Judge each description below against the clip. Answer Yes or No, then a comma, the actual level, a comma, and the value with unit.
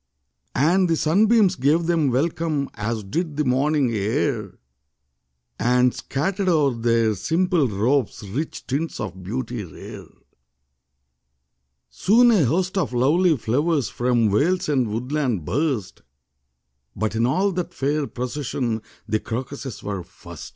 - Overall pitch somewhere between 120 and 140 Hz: Yes, low, 135 Hz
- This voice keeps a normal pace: No, slow, 125 wpm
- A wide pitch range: Yes, wide, 6.0 semitones